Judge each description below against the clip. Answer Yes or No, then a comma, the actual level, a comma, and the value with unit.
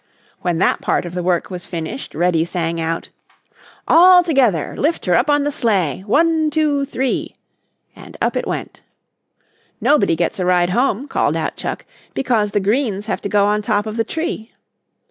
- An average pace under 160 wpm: No, average, 175 wpm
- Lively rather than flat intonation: Yes, wide, 7.9 semitones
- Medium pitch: No, high, 210 Hz